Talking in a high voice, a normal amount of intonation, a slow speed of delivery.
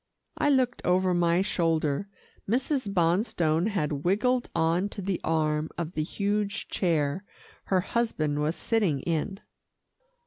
No: medium, 180 Hz; average, 4.5 semitones; slow, 130 wpm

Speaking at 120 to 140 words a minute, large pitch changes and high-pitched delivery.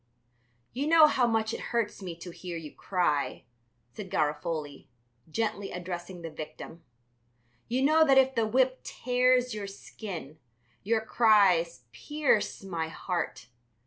Yes: slow, 135 wpm; wide, 6.6 semitones; high, 200 Hz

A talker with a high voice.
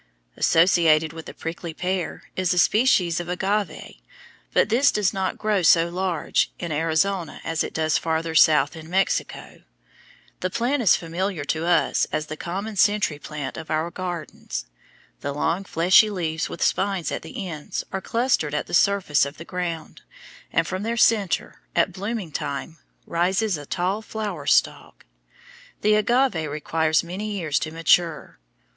No: medium, 175 Hz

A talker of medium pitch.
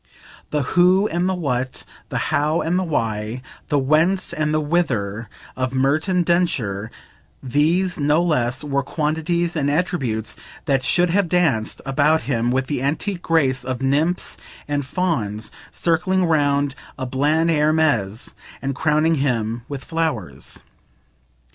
Yes: medium, 145 Hz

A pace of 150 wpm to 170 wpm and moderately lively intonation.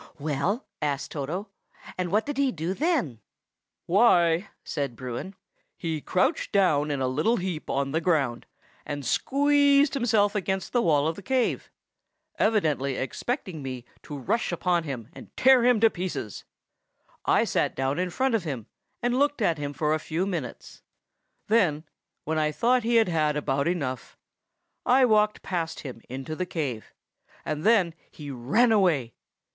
No: average, 160 wpm; wide, 7.4 semitones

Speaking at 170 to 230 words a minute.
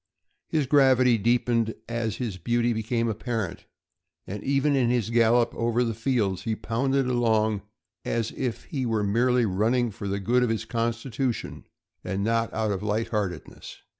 No: average, 160 wpm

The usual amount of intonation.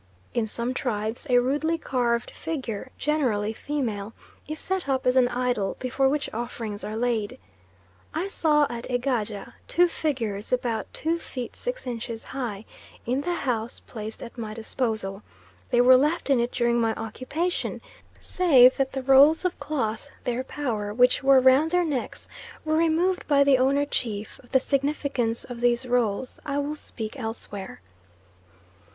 Yes: average, 4.1 semitones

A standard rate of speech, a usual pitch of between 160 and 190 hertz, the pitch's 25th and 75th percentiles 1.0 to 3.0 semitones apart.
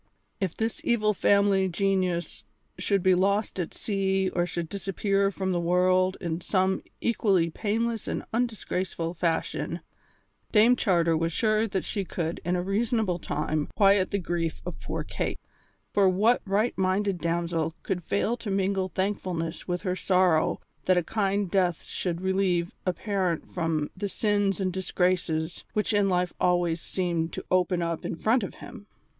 Yes: average, 160 wpm; medium, 185 Hz; narrow, 2.5 semitones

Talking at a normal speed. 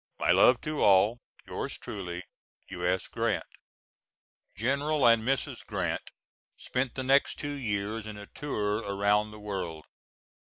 No: slow, 130 wpm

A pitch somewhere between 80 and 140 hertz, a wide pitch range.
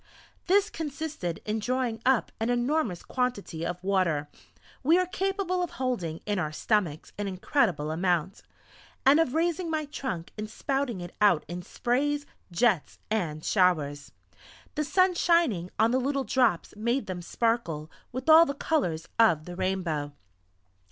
No: high, 225 Hz; wide, 8.3 semitones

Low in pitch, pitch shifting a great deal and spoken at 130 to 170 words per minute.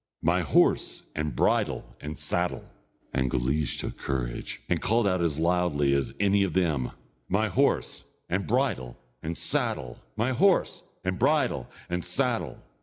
Yes: very low, 85 Hz; wide, 5.9 semitones; average, 145 wpm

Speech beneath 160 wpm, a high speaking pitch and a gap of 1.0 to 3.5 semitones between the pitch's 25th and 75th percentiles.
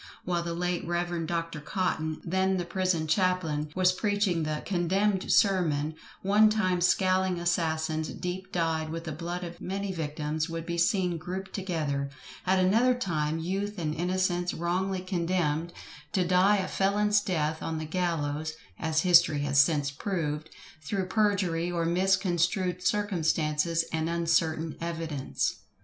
No: average, 140 wpm; medium, 175 Hz; average, 2.8 semitones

